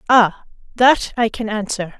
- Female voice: Yes, female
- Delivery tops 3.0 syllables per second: Yes, 4.2 syllables/s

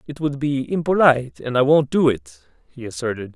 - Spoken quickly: No, average, 195 wpm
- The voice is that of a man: Yes, male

